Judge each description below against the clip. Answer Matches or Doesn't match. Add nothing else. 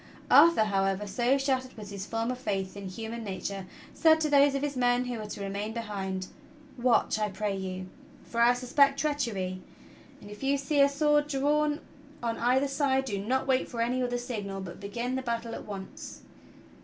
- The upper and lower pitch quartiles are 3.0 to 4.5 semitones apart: Doesn't match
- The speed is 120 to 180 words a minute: Doesn't match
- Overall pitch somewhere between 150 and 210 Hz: Doesn't match